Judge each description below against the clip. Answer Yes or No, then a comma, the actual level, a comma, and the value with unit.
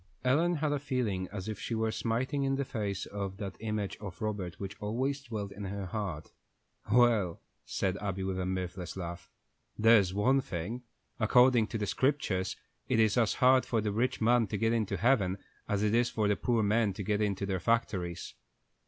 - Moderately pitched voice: No, low, 105 Hz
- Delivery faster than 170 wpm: Yes, average, 190 wpm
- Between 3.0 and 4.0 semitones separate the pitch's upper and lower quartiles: Yes, average, 3.7 semitones